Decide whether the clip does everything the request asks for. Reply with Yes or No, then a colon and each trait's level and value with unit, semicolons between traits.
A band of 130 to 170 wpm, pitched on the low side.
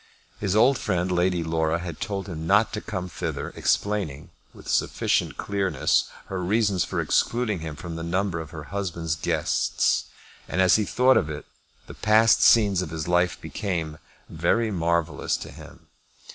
Yes: average, 160 wpm; very low, 90 Hz